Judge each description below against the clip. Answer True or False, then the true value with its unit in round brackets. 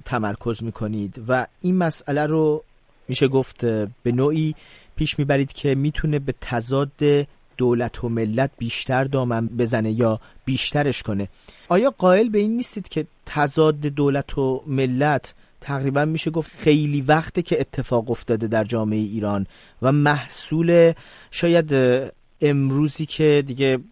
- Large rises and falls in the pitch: False (4.0 semitones)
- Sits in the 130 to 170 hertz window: True (135 Hz)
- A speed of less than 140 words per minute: True (130 wpm)